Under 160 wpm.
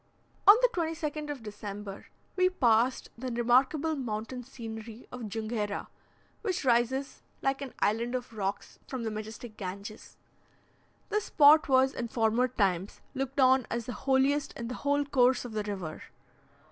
Yes: average, 150 wpm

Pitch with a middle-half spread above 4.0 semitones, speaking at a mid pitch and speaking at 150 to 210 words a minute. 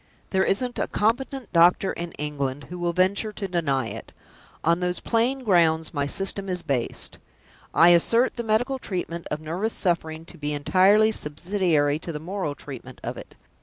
Yes: average, 4.8 semitones; medium, 175 Hz; average, 170 wpm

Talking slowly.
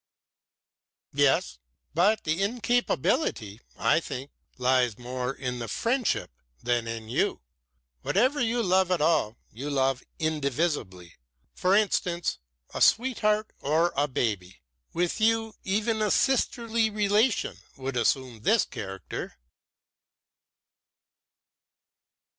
Yes: slow, 105 wpm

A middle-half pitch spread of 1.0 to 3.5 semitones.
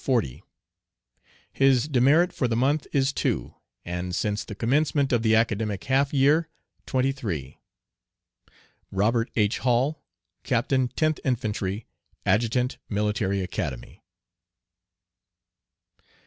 No: average, 4.6 semitones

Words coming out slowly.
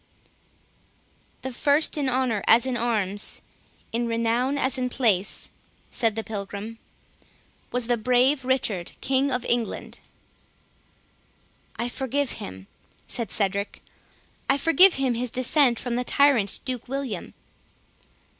Yes: slow, 120 wpm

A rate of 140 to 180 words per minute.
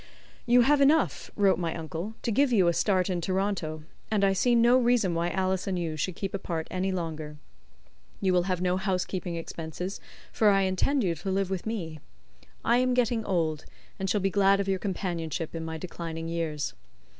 No: average, 195 wpm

